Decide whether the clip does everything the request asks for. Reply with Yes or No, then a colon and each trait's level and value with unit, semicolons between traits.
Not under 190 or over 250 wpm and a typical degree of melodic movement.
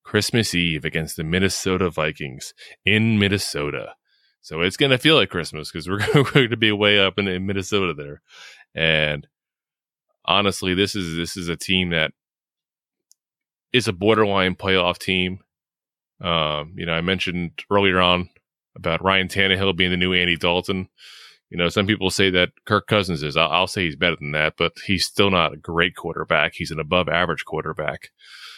No: average, 175 wpm; average, 3.0 semitones